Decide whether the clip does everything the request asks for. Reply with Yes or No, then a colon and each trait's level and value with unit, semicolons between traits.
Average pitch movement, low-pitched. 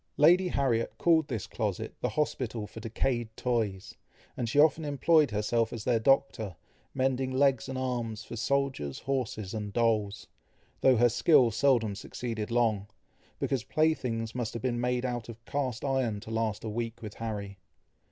Yes: average, 3.3 semitones; low, 120 Hz